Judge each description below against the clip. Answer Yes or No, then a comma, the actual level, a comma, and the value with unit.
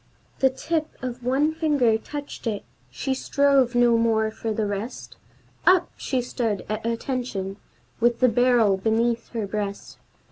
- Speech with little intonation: No, average, 3.3 semitones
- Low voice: No, high, 240 Hz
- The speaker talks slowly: No, average, 150 wpm